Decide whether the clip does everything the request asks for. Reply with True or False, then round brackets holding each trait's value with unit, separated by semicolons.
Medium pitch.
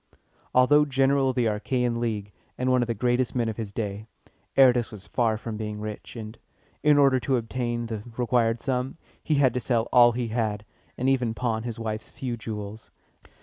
False (120 Hz)